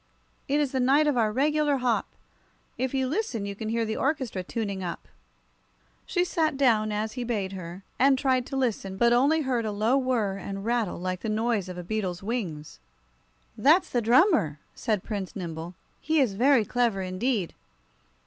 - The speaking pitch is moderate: No, high, 230 Hz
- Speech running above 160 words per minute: Yes, average, 180 wpm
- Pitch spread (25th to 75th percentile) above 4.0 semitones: Yes, average, 5.2 semitones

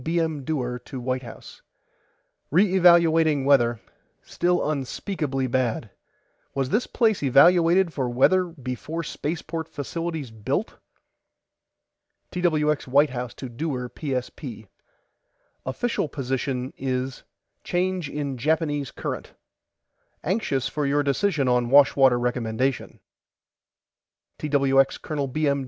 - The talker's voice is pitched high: No, medium, 140 Hz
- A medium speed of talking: No, slow, 110 wpm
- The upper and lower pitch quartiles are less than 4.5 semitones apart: Yes, average, 4.1 semitones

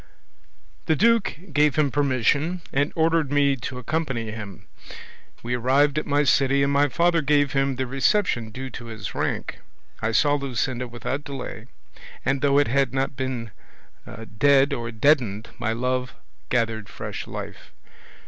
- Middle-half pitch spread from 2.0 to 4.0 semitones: Yes, average, 3.1 semitones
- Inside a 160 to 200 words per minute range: No, average, 150 wpm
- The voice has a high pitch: No, low, 135 Hz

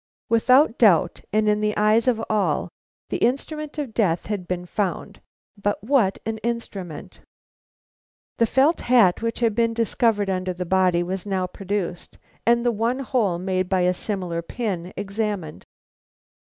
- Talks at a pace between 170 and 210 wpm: No, average, 155 wpm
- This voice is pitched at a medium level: No, high, 210 Hz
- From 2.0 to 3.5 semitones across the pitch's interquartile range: No, average, 4.0 semitones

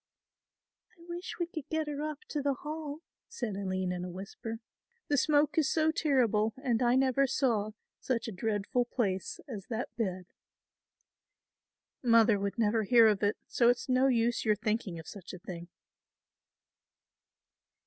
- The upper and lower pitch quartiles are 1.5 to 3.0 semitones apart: No, average, 5.2 semitones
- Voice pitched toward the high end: Yes, high, 235 Hz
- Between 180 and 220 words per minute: No, average, 160 wpm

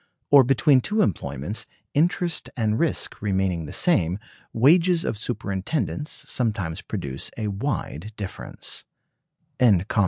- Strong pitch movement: Yes, wide, 7.5 semitones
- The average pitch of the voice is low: Yes, low, 110 Hz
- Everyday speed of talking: No, slow, 105 wpm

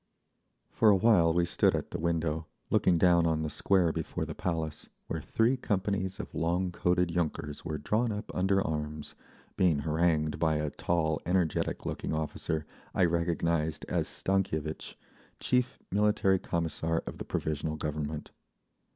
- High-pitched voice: No, very low, 85 Hz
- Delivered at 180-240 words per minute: No, average, 150 wpm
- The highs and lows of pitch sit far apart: No, average, 3.1 semitones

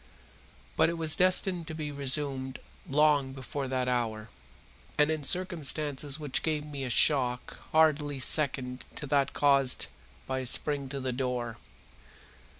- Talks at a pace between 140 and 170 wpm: Yes, average, 145 wpm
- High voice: No, medium, 140 Hz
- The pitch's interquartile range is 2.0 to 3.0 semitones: Yes, average, 2.7 semitones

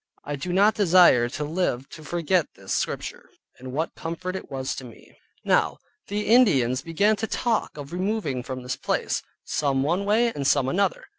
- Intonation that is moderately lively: No, wide, 7.0 semitones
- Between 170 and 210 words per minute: Yes, average, 180 wpm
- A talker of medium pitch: Yes, medium, 165 Hz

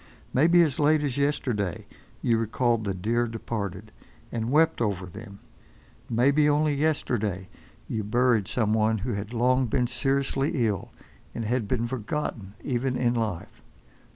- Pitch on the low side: Yes, low, 120 Hz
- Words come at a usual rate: Yes, average, 145 wpm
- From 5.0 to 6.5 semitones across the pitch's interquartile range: No, average, 4.2 semitones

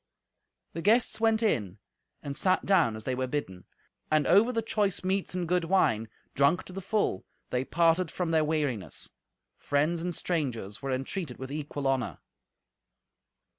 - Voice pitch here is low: No, medium, 160 Hz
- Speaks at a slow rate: No, average, 160 wpm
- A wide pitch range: Yes, wide, 5.9 semitones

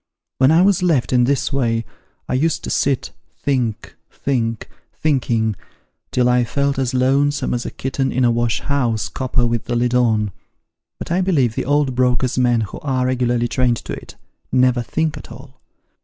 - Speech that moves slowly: No, average, 180 wpm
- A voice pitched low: Yes, low, 125 Hz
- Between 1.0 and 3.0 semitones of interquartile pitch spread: Yes, narrow, 2.6 semitones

